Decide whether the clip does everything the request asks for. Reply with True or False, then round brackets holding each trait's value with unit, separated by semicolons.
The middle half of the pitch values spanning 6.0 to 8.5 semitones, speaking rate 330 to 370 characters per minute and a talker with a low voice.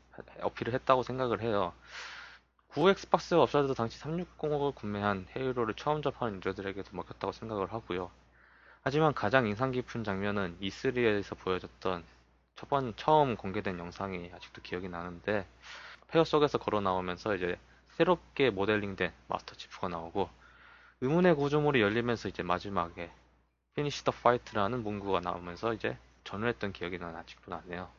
True (6.4 semitones; 355 characters per minute; 100 Hz)